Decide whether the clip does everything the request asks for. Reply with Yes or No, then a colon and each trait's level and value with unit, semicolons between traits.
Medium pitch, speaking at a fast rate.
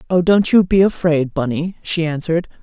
No: medium, 170 Hz; average, 185 wpm